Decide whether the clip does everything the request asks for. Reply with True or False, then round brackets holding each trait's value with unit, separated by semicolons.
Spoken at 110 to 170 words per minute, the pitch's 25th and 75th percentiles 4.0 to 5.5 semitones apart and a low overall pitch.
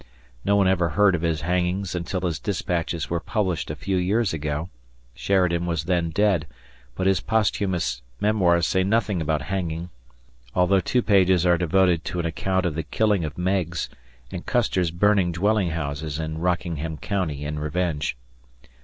False (160 wpm; 2.9 semitones; 90 Hz)